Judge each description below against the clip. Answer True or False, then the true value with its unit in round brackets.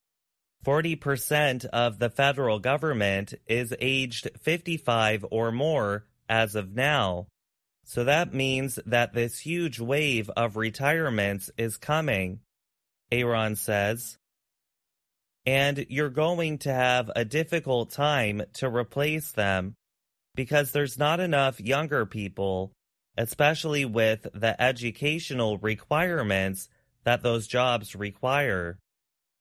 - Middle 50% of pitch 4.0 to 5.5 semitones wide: True (4.7 semitones)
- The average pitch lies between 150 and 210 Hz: False (120 Hz)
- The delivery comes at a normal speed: False (105 wpm)